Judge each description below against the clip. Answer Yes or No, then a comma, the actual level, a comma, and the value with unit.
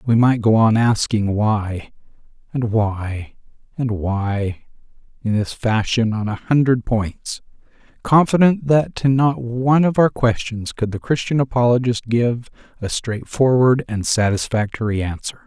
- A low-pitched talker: Yes, low, 115 Hz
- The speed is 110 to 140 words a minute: Yes, slow, 135 wpm